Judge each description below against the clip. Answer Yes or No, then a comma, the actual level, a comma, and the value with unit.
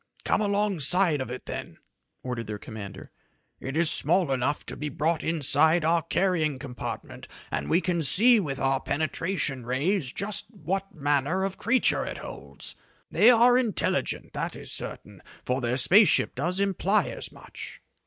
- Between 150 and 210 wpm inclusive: Yes, average, 160 wpm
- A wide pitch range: Yes, wide, 6.3 semitones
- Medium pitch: Yes, medium, 160 Hz